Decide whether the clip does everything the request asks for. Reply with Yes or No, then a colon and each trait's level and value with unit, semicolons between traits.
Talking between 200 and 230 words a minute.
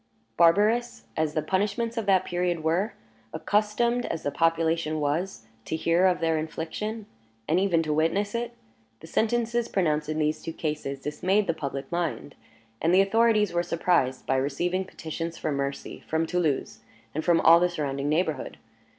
No: average, 165 wpm